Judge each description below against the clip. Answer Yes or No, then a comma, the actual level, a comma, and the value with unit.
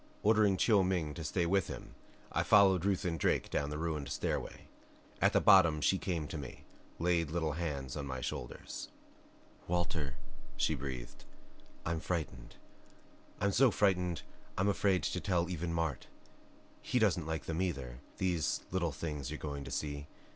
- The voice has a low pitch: Yes, very low, 85 Hz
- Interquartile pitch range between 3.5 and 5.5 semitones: Yes, average, 3.9 semitones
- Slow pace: No, average, 160 wpm